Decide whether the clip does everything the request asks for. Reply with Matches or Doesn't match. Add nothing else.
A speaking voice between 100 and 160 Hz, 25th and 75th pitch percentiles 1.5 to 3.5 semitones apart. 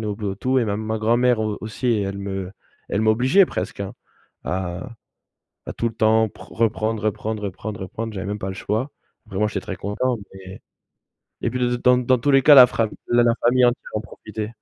Matches